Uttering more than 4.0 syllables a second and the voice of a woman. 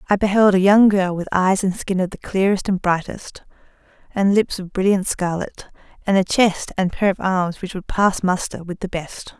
Yes: 4.8 syllables/s; female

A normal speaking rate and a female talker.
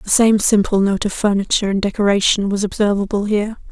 Yes: average, 180 wpm; female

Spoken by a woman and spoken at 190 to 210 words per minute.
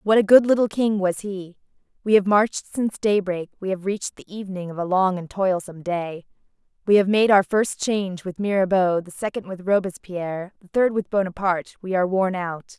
Yes: female; average, 200 wpm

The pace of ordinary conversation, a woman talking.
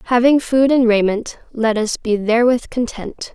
Yes: average, 160 wpm; female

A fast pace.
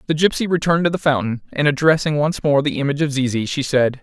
Yes: fast, 240 wpm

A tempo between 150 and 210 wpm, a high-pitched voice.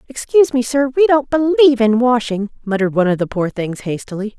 Yes: fast, 205 wpm; high, 240 Hz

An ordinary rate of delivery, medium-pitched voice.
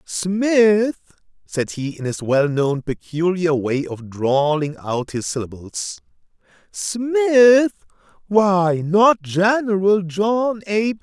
No: slow, 110 wpm; medium, 180 Hz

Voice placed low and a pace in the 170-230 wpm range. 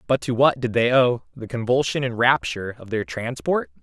Yes: low, 115 Hz; fast, 205 wpm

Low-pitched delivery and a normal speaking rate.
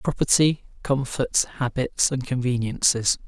No: low, 130 Hz; slow, 90 wpm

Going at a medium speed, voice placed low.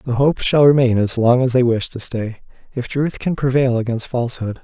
No: fast, 220 wpm; low, 125 Hz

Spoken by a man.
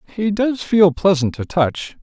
Yes: male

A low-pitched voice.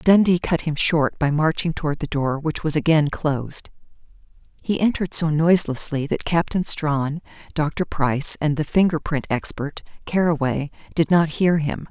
No: medium, 155 Hz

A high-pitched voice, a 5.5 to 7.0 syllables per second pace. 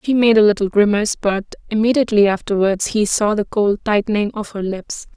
Yes: high, 210 Hz; 5.6 syllables/s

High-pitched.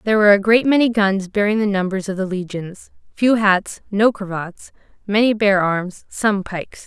Yes: high, 200 Hz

